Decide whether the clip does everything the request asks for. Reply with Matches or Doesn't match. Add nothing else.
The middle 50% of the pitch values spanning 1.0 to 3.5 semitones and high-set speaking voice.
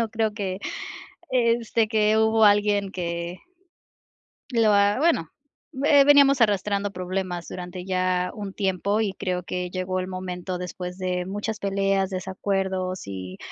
Matches